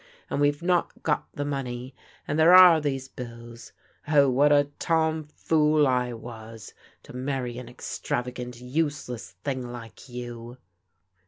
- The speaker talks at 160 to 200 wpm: No, average, 145 wpm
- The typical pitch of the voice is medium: No, low, 130 Hz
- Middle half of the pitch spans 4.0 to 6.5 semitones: No, average, 3.3 semitones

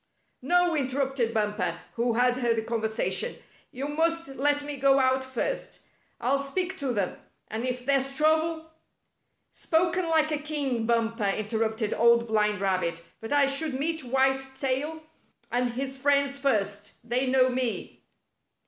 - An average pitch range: Yes, average, 3.9 semitones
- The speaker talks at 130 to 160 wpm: Yes, average, 150 wpm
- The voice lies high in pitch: Yes, very high, 265 Hz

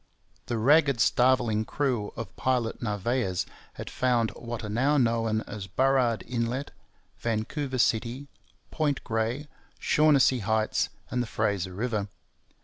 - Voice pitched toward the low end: Yes, low, 120 Hz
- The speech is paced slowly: Yes, slow, 125 wpm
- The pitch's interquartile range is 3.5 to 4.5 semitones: No, average, 3.0 semitones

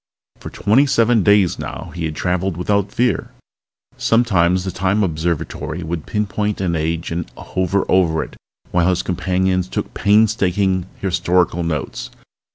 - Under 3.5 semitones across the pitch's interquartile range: Yes, average, 2.9 semitones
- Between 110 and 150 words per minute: Yes, average, 140 wpm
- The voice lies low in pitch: Yes, very low, 95 Hz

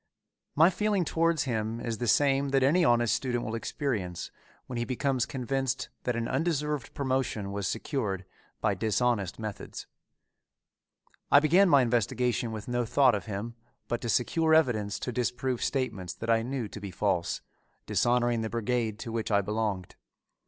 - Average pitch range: Yes, average, 3.7 semitones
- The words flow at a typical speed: Yes, average, 160 wpm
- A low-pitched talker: Yes, low, 120 Hz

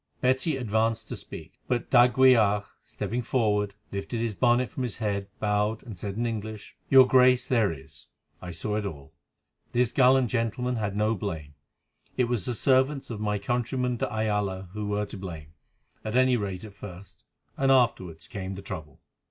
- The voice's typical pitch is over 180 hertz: No, low, 110 Hz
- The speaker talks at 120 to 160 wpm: No, average, 175 wpm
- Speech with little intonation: No, average, 3.7 semitones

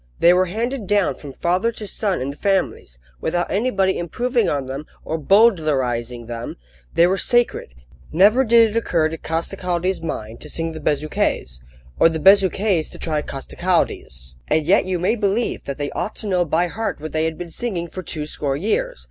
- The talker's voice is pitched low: No, medium, 175 Hz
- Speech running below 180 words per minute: No, average, 190 wpm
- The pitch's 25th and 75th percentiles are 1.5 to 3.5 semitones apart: No, average, 5.1 semitones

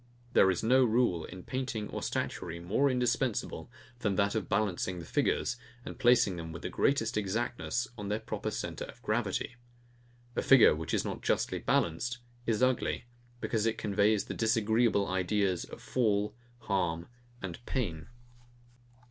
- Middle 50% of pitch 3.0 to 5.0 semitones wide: Yes, average, 4.3 semitones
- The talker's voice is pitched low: Yes, low, 105 Hz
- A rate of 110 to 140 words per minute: No, average, 155 wpm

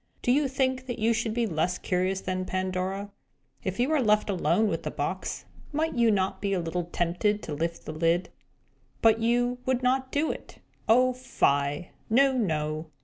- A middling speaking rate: Yes, average, 185 wpm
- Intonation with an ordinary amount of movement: No, wide, 5.7 semitones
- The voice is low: No, high, 210 Hz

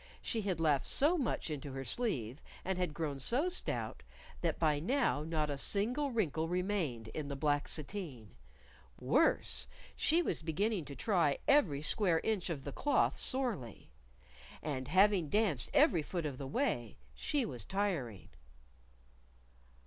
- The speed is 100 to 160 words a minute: Yes, average, 150 wpm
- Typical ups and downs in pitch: No, wide, 6.9 semitones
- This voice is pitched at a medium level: Yes, medium, 165 Hz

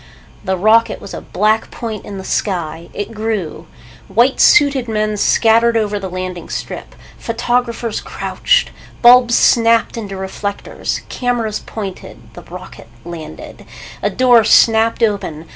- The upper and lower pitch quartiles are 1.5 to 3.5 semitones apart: Yes, average, 3.1 semitones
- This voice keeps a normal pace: No, slow, 130 wpm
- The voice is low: No, high, 220 Hz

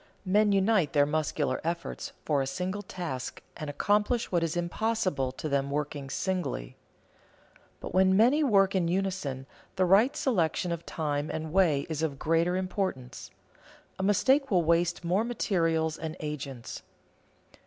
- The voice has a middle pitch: Yes, medium, 170 Hz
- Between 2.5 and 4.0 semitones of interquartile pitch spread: No, average, 4.4 semitones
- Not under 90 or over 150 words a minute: Yes, average, 145 wpm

